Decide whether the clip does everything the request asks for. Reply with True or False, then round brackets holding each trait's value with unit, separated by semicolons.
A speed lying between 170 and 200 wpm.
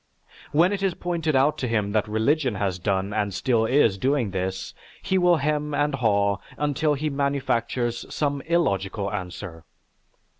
False (155 wpm)